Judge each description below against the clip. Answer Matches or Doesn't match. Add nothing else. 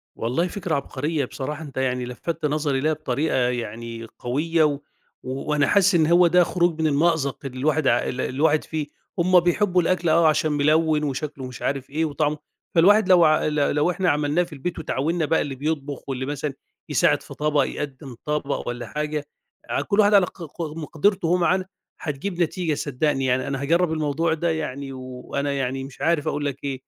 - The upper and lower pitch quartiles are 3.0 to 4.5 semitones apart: Matches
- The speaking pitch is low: Doesn't match